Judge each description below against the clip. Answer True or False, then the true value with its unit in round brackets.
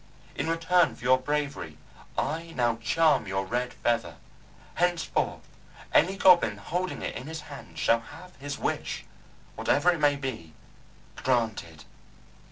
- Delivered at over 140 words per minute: False (135 wpm)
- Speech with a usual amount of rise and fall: False (5.9 semitones)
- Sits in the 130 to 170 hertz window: True (140 Hz)